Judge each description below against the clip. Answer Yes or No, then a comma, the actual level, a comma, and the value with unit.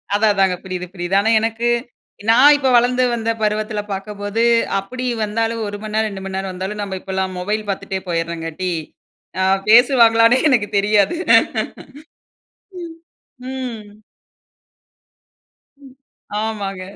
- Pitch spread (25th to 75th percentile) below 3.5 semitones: Yes, average, 3.0 semitones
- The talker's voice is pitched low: No, high, 210 Hz